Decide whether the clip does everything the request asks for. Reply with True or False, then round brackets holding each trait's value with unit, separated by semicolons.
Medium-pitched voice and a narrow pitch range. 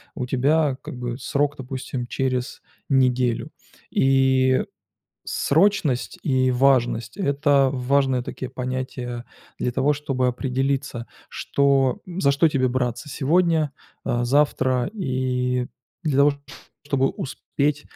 False (130 Hz; 2.0 semitones)